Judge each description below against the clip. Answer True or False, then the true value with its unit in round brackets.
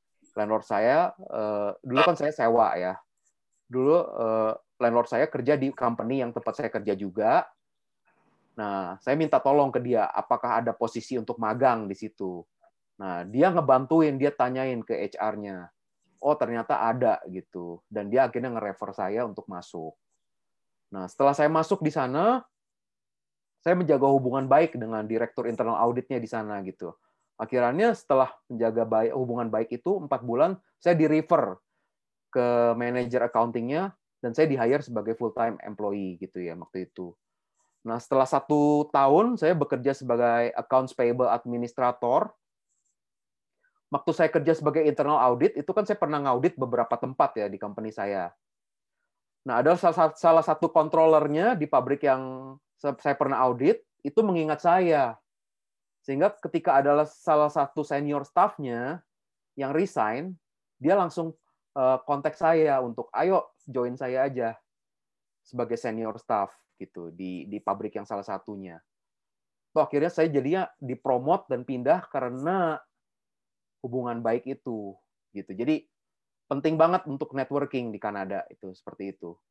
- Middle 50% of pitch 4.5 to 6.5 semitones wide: True (5.2 semitones)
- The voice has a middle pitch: False (130 Hz)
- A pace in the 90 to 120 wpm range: False (135 wpm)